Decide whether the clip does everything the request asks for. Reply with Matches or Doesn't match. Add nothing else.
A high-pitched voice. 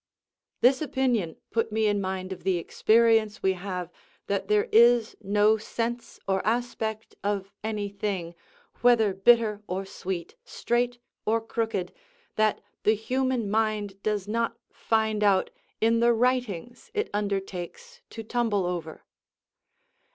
Matches